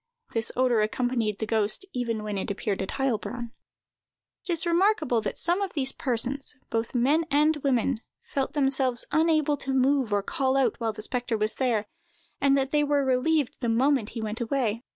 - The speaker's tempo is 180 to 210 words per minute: Yes, average, 185 wpm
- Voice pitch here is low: No, very high, 255 Hz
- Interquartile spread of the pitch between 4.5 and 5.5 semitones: No, average, 3.8 semitones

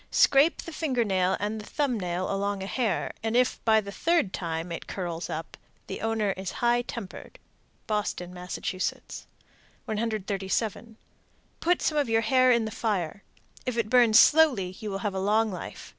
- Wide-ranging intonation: No, average, 4.0 semitones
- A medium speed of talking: Yes, average, 175 wpm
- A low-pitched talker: No, high, 215 Hz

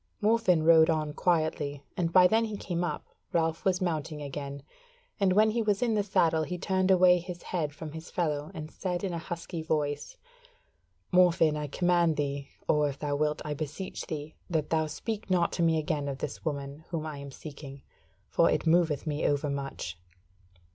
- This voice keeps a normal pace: Yes, average, 190 wpm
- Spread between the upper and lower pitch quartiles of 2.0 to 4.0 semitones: Yes, average, 3.3 semitones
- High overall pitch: No, medium, 160 Hz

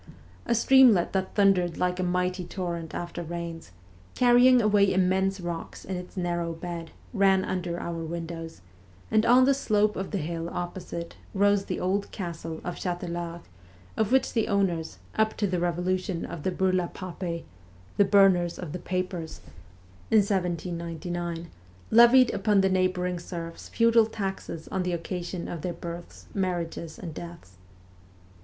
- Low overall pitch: No, medium, 180 Hz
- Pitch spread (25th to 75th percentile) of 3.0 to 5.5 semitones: No, narrow, 2.5 semitones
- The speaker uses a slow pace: No, average, 150 wpm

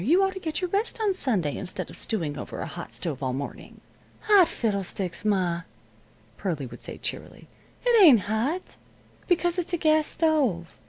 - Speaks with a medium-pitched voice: No, high, 240 Hz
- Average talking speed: Yes, average, 175 wpm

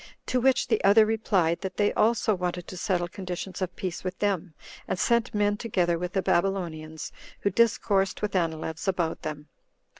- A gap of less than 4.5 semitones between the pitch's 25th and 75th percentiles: Yes, average, 3.1 semitones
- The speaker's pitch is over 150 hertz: Yes, medium, 185 Hz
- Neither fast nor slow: Yes, average, 175 wpm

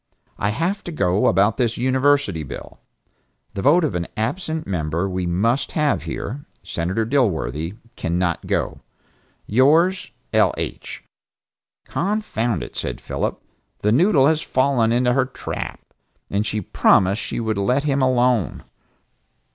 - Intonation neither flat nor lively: No, wide, 6.6 semitones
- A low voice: Yes, low, 120 Hz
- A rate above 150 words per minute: No, slow, 135 wpm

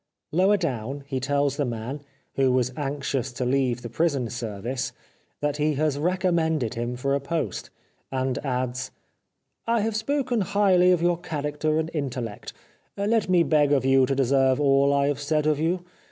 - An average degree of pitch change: Yes, average, 4.1 semitones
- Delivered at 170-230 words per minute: Yes, average, 180 wpm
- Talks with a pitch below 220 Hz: Yes, medium, 140 Hz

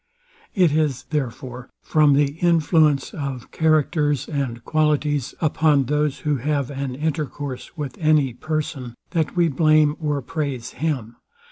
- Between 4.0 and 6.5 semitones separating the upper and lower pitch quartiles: No, narrow, 2.5 semitones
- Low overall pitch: No, medium, 145 Hz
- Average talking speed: No, slow, 130 wpm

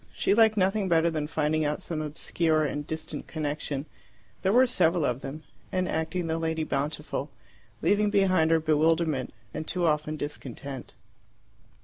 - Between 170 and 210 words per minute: No, average, 150 wpm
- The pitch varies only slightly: No, average, 3.1 semitones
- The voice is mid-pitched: Yes, medium, 160 Hz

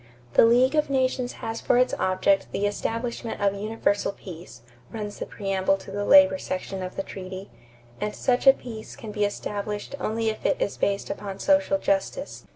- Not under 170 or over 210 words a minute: Yes, average, 180 wpm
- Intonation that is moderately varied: Yes, average, 3.9 semitones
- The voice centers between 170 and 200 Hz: No, high, 210 Hz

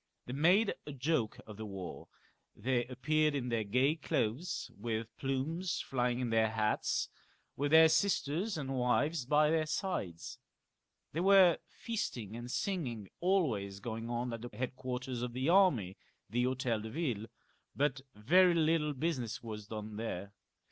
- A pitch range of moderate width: No, wide, 5.7 semitones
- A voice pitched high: No, low, 130 Hz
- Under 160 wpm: Yes, average, 150 wpm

